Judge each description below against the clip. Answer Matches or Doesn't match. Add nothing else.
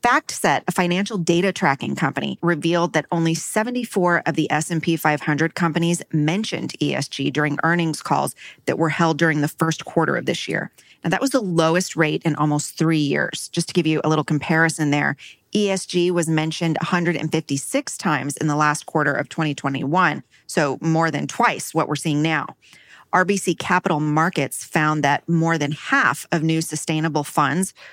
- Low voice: Doesn't match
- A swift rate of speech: Doesn't match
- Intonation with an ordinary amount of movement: Doesn't match